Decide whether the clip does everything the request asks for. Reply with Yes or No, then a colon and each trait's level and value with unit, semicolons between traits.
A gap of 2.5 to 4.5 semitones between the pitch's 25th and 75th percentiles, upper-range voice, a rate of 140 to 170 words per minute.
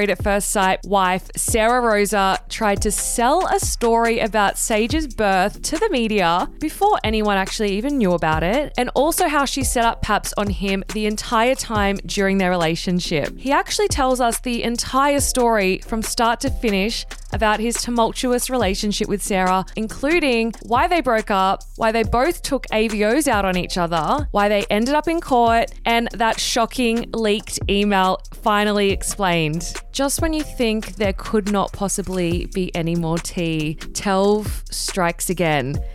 Yes: average, 3.8 semitones; high, 215 Hz; average, 165 wpm